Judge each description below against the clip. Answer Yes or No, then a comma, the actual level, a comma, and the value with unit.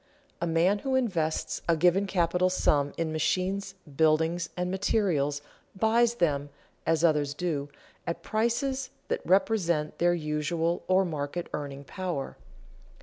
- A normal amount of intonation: Yes, average, 3.7 semitones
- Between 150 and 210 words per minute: No, slow, 135 wpm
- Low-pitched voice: No, medium, 170 Hz